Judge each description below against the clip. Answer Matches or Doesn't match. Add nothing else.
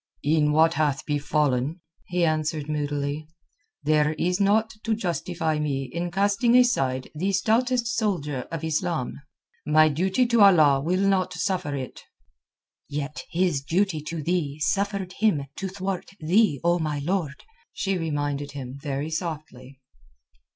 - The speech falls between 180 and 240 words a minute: Doesn't match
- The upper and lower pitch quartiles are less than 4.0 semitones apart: Doesn't match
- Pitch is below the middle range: Doesn't match